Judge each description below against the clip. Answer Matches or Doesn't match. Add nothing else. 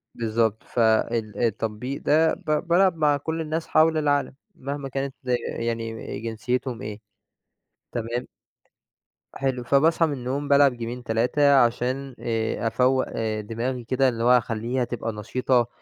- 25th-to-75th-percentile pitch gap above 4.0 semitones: Doesn't match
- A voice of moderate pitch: Doesn't match